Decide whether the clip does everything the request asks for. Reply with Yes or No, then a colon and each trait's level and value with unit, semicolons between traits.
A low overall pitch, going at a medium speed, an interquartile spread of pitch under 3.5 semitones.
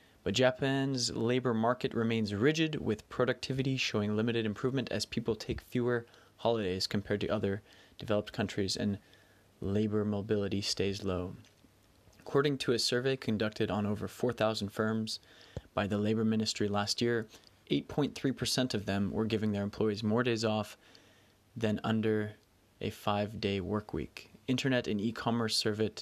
Yes: low, 110 Hz; average, 145 wpm; narrow, 2.4 semitones